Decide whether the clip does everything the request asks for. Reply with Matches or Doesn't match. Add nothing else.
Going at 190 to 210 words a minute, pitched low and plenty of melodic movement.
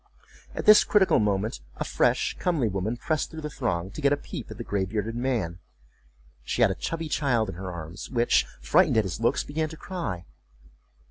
Matches